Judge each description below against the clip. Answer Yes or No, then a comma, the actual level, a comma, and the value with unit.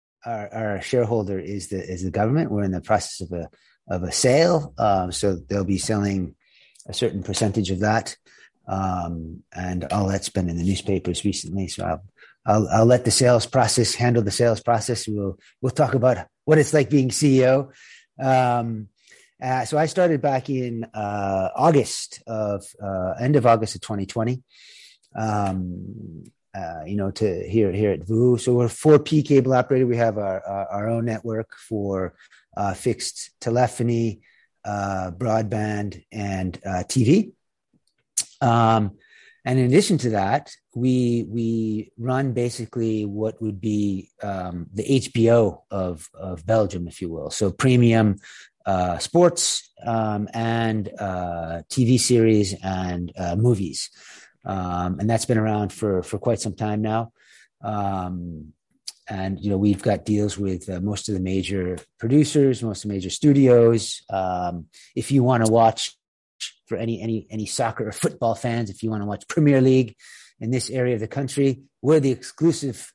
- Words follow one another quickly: No, average, 165 wpm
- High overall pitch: No, low, 110 Hz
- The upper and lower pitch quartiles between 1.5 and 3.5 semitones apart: No, average, 3.9 semitones